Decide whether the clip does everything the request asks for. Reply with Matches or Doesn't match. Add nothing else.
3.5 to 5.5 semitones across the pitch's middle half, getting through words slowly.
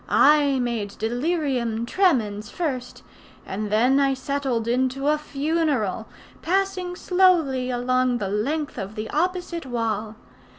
Matches